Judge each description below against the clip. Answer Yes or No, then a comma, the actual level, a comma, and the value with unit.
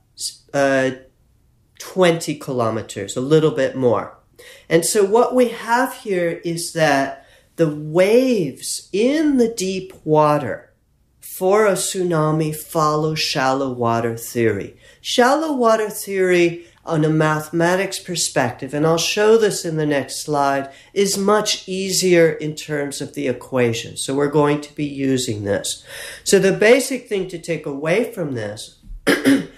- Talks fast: No, slow, 135 wpm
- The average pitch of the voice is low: No, medium, 155 Hz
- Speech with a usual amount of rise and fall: No, wide, 5.8 semitones